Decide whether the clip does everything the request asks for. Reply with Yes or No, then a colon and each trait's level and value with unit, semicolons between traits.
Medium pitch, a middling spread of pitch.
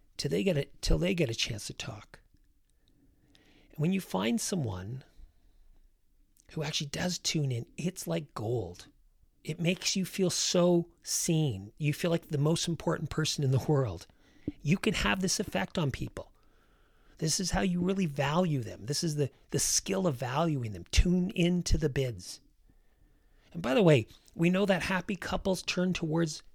Yes: medium, 165 Hz; average, 4.9 semitones